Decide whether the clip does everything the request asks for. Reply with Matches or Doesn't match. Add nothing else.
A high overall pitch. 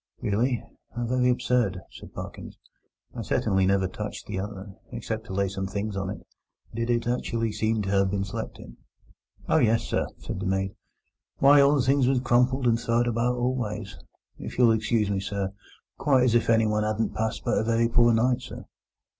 Doesn't match